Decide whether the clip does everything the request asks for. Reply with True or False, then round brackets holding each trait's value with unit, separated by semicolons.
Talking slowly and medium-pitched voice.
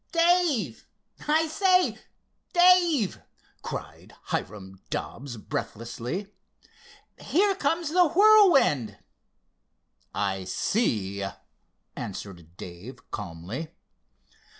True (70 wpm; 165 Hz)